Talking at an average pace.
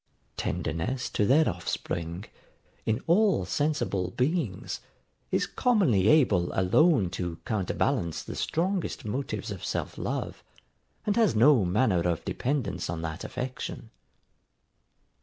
No: slow, 120 wpm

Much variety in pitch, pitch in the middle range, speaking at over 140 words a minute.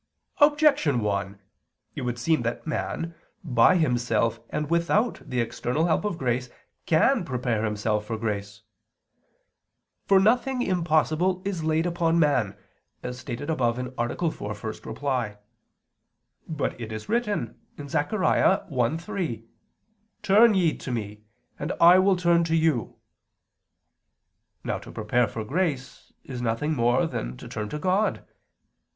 No: wide, 6.9 semitones; medium, 145 Hz; slow, 135 wpm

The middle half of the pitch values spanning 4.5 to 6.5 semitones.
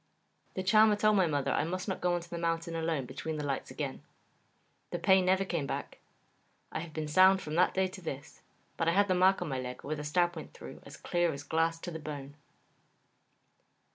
No: average, 3.4 semitones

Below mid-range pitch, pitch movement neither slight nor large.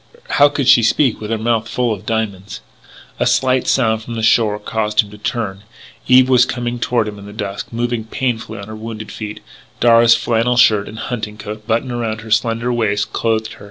No: low, 115 Hz; narrow, 2.1 semitones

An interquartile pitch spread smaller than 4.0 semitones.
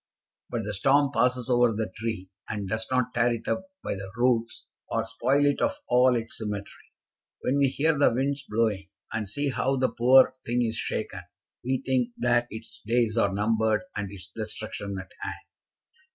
Yes: average, 3.0 semitones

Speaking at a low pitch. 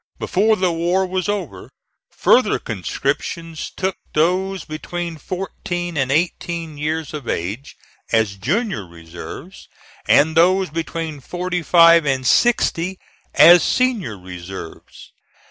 No: medium, 165 Hz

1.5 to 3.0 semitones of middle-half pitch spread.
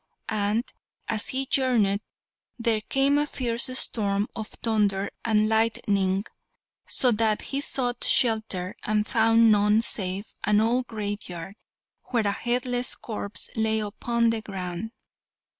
Yes: narrow, 2.5 semitones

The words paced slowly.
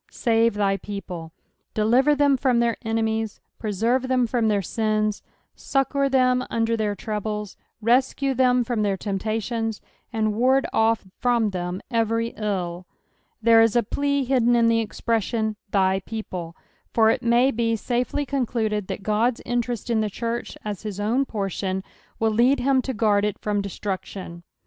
No: average, 160 wpm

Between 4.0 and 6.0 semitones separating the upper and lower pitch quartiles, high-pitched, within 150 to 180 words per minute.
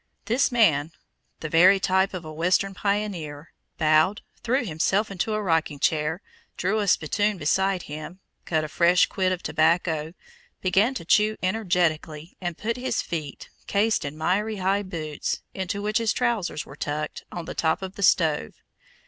No: average, 4.4 semitones; medium, 180 Hz; average, 165 wpm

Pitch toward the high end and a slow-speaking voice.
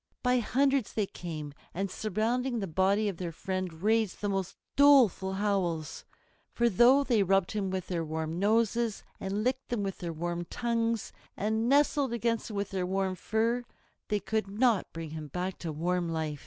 No: high, 200 Hz; average, 180 wpm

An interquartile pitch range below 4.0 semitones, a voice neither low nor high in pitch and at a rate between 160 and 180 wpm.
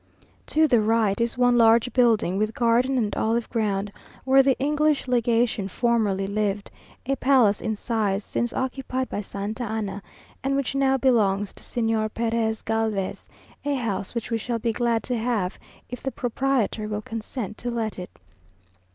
No: average, 2.8 semitones; high, 230 Hz; average, 165 wpm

